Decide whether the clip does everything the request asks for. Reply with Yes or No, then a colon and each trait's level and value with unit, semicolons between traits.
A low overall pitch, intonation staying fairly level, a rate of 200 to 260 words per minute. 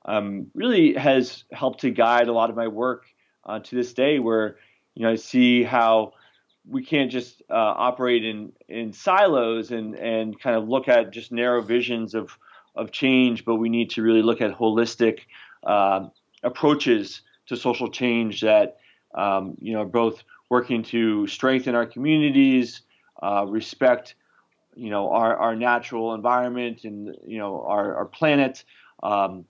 No: low, 120 Hz; narrow, 2.3 semitones; average, 160 wpm